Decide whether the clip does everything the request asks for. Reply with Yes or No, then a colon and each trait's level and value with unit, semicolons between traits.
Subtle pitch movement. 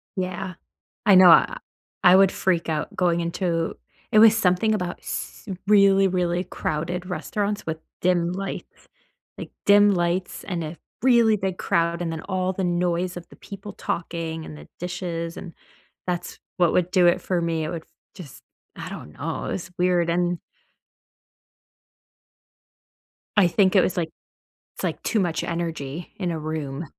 Yes: narrow, 2.1 semitones